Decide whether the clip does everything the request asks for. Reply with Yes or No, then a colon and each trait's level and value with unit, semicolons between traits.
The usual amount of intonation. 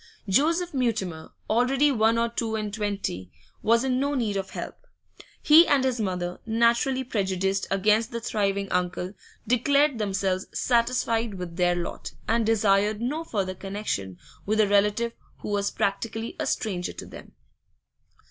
Yes: average, 3.4 semitones